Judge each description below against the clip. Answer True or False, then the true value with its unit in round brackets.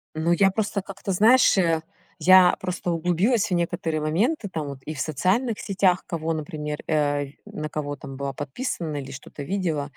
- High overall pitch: False (165 Hz)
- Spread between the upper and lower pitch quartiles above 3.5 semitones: True (4.3 semitones)